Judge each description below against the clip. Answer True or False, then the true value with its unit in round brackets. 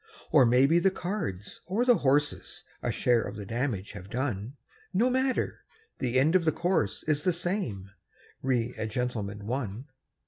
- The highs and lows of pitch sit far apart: True (8.2 semitones)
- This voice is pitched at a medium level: False (130 Hz)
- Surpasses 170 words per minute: False (165 wpm)